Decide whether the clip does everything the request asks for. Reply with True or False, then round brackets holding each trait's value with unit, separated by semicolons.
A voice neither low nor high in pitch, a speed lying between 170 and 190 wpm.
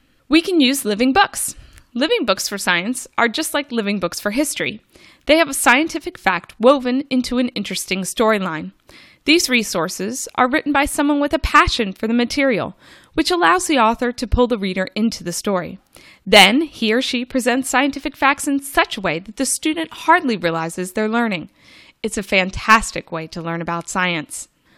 False (245 Hz; 180 wpm)